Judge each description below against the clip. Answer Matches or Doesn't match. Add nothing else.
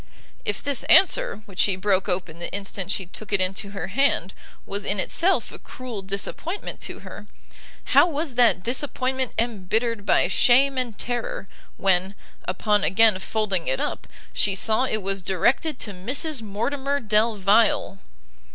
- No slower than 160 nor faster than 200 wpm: Doesn't match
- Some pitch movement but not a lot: Matches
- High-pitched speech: Matches